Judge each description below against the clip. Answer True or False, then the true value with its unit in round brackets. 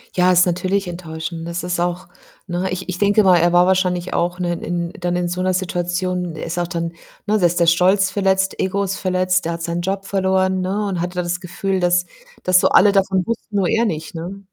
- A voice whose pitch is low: False (180 Hz)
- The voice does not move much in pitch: True (1.5 semitones)